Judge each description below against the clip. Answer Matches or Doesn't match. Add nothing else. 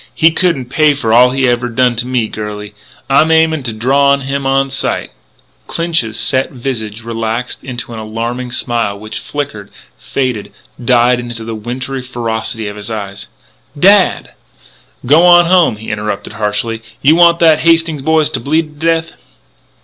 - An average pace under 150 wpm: Doesn't match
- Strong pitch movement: Doesn't match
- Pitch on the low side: Matches